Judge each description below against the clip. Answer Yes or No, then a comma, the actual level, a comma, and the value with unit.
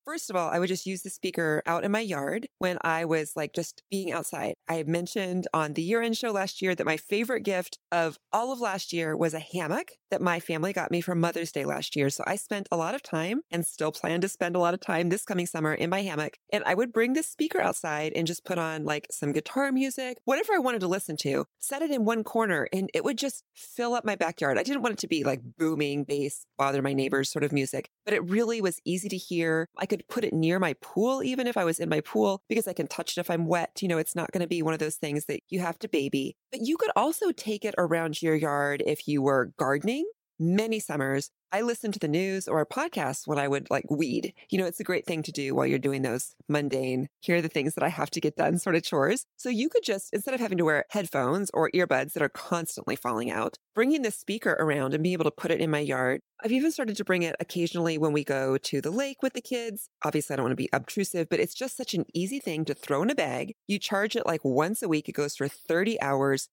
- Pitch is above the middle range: No, medium, 175 Hz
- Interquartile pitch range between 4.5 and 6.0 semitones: Yes, wide, 5.4 semitones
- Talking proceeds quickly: Yes, fast, 265 wpm